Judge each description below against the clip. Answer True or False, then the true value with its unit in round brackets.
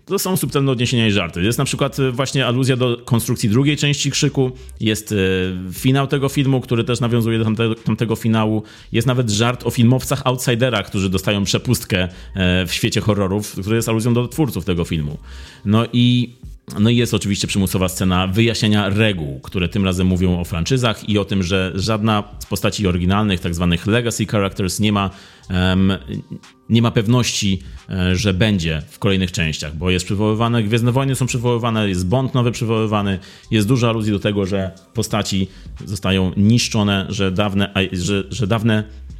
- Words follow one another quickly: True (170 wpm)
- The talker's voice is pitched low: True (105 Hz)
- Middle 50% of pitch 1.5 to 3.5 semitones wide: False (4.1 semitones)